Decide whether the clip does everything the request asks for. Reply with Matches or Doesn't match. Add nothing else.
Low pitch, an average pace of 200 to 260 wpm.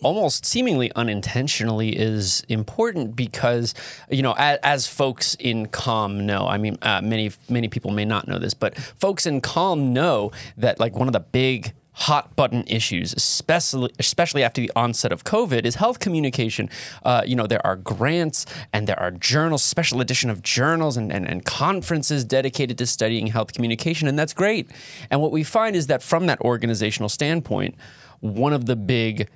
Doesn't match